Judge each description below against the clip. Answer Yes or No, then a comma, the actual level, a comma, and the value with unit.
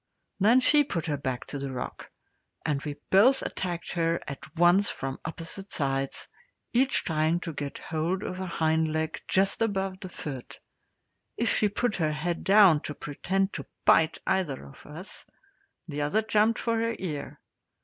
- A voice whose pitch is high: No, medium, 170 Hz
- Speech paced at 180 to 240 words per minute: No, average, 170 wpm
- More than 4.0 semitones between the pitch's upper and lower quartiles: Yes, average, 4.7 semitones